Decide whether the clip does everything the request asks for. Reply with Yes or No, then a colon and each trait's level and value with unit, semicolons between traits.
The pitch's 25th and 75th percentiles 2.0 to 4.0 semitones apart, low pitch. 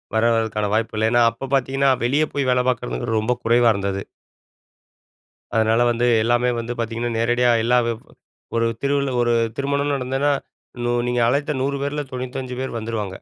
Yes: average, 3.0 semitones; low, 120 Hz